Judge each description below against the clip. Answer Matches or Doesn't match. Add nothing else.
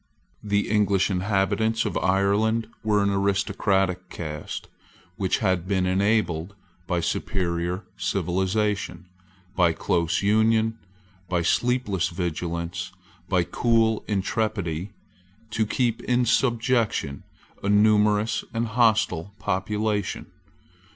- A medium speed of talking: Doesn't match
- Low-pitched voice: Matches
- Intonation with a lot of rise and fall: Doesn't match